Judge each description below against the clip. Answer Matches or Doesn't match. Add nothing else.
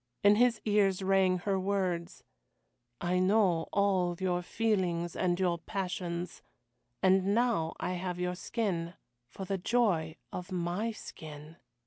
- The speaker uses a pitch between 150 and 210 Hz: Matches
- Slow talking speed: Matches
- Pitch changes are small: Matches